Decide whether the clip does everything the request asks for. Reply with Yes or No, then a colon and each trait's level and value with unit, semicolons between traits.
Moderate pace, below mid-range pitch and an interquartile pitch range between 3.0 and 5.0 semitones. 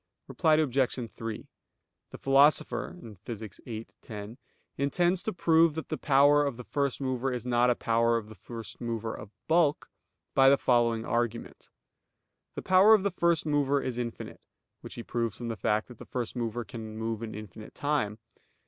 Yes: average, 175 wpm; low, 120 Hz; average, 4.0 semitones